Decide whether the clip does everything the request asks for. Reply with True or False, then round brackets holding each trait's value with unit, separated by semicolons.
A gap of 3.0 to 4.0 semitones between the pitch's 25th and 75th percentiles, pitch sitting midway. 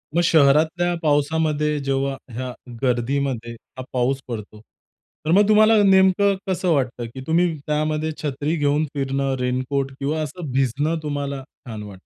True (3.4 semitones; 145 Hz)